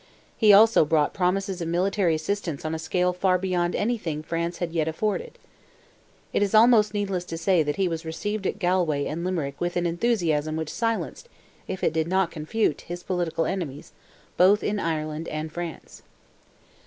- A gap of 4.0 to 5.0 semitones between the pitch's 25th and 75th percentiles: No, average, 3.5 semitones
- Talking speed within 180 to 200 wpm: No, average, 170 wpm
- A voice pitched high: No, medium, 175 Hz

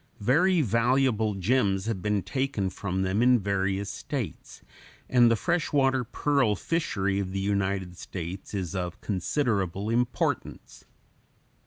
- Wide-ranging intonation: No, average, 4.7 semitones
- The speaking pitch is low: Yes, low, 100 Hz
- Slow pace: Yes, slow, 130 wpm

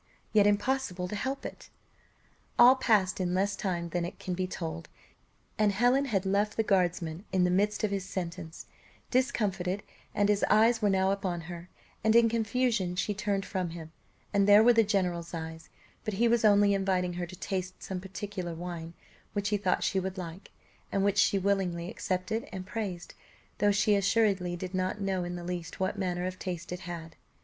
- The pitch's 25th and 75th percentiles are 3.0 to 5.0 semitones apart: No, narrow, 2.5 semitones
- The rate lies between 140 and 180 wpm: No, average, 190 wpm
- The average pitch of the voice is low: No, high, 190 Hz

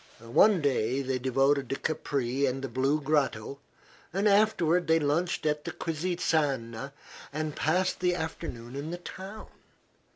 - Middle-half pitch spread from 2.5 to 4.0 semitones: No, average, 4.5 semitones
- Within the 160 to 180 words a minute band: No, average, 140 wpm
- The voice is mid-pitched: Yes, medium, 150 Hz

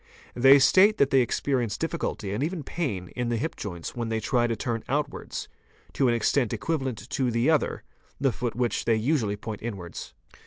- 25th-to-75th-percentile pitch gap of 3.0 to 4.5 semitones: Yes, average, 3.9 semitones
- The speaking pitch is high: No, low, 120 Hz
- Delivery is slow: No, average, 195 wpm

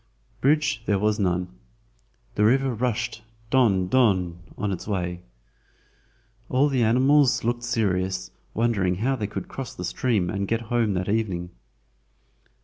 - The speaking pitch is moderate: No, low, 110 Hz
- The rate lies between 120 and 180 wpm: Yes, average, 140 wpm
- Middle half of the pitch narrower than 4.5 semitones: No, average, 4.9 semitones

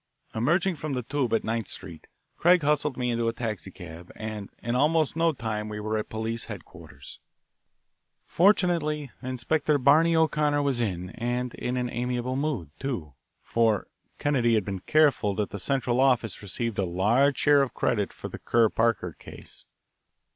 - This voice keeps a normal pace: Yes, average, 160 wpm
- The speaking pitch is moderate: No, low, 120 Hz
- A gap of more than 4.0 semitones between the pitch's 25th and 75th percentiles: Yes, average, 5.2 semitones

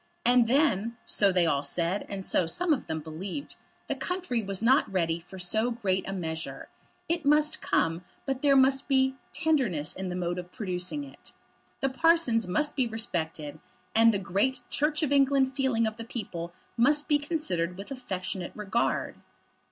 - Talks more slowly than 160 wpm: No, average, 175 wpm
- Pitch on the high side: Yes, high, 225 Hz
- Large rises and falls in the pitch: Yes, wide, 7.2 semitones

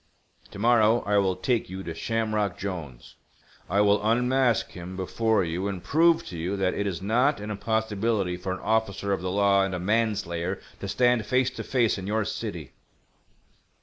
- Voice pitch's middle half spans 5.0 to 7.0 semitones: No, average, 3.1 semitones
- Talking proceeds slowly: No, average, 180 wpm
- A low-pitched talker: Yes, low, 100 Hz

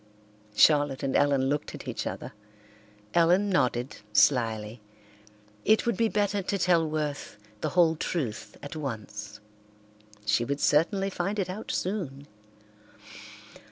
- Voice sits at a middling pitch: Yes, medium, 150 Hz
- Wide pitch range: Yes, wide, 5.8 semitones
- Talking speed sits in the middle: No, slow, 125 wpm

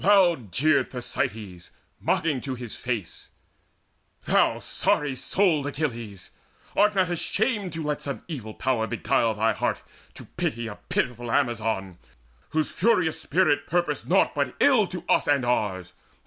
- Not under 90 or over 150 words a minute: Yes, average, 145 wpm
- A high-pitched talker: No, low, 135 Hz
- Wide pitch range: Yes, wide, 7.1 semitones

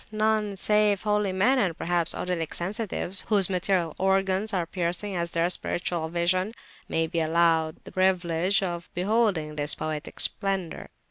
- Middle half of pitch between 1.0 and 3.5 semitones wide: Yes, average, 2.9 semitones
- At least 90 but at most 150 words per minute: Yes, average, 145 wpm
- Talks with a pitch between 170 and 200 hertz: Yes, medium, 185 Hz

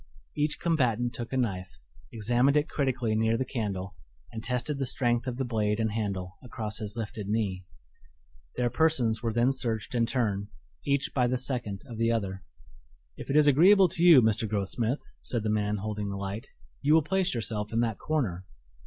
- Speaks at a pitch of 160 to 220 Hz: No, low, 115 Hz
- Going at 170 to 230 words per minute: Yes, average, 190 wpm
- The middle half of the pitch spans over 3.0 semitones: Yes, average, 3.8 semitones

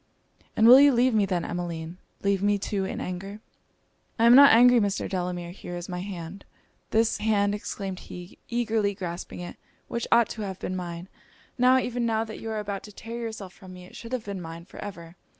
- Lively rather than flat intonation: No, average, 4.0 semitones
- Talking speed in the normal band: No, fast, 210 wpm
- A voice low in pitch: No, high, 200 Hz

